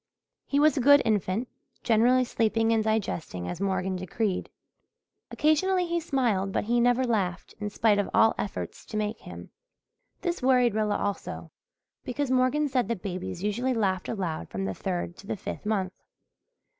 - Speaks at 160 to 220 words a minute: Yes, average, 170 wpm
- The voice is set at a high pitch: Yes, high, 220 Hz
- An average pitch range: Yes, average, 4.8 semitones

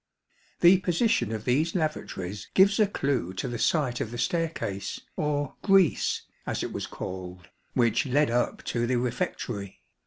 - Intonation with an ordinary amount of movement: No, wide, 7.0 semitones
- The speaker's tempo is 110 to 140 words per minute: No, average, 160 wpm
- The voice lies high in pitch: No, low, 130 Hz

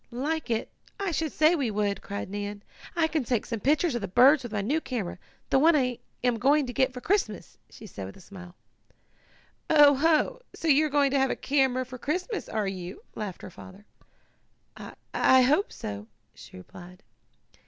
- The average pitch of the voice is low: No, very high, 255 Hz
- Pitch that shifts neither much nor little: No, wide, 6.7 semitones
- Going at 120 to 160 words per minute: No, average, 195 wpm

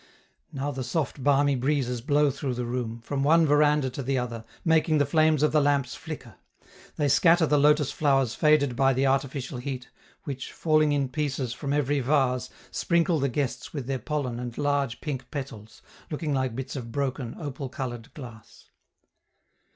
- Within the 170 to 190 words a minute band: Yes, average, 175 wpm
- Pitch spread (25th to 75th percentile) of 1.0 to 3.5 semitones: Yes, average, 2.8 semitones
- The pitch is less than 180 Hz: Yes, medium, 140 Hz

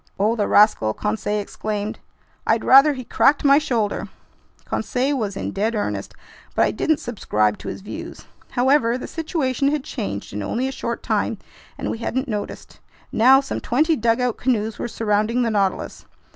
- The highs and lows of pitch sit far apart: No, average, 4.2 semitones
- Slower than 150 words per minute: No, average, 170 wpm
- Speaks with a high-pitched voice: Yes, high, 235 Hz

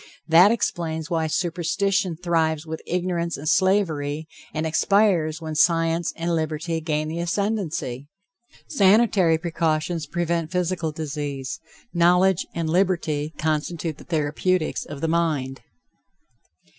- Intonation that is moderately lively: No, narrow, 2.3 semitones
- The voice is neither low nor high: Yes, medium, 165 Hz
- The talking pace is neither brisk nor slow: No, slow, 115 wpm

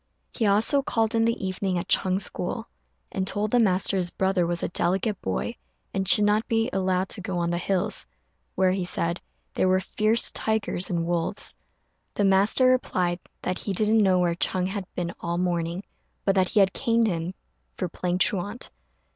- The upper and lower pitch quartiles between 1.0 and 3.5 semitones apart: Yes, average, 2.9 semitones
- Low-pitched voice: No, high, 190 Hz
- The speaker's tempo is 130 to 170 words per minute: No, average, 190 wpm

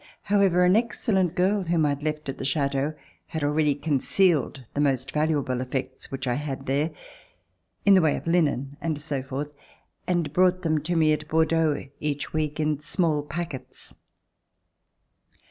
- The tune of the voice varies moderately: Yes, average, 3.1 semitones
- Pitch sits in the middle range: Yes, medium, 150 Hz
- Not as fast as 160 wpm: No, average, 165 wpm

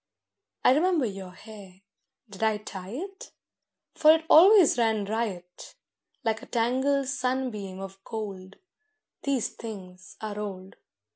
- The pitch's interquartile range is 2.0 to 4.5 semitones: No, average, 5.3 semitones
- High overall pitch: Yes, high, 220 Hz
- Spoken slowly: Yes, slow, 120 wpm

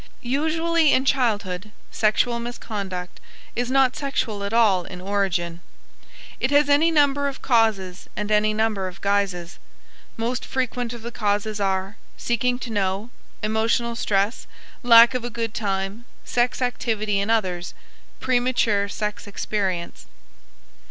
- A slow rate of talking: Yes, slow, 130 wpm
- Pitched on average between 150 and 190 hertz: No, high, 220 Hz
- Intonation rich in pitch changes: No, average, 3.6 semitones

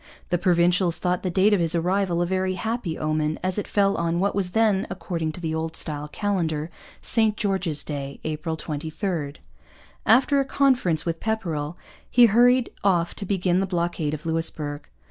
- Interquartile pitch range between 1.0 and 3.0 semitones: No, average, 3.8 semitones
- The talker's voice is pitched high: No, medium, 175 Hz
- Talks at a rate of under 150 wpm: No, average, 175 wpm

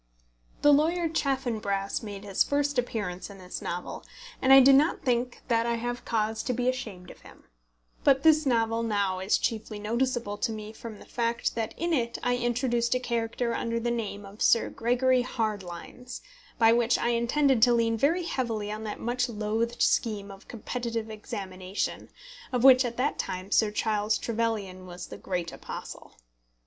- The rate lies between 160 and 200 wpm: Yes, average, 175 wpm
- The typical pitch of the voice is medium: No, high, 230 Hz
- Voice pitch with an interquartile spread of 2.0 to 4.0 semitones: Yes, average, 2.9 semitones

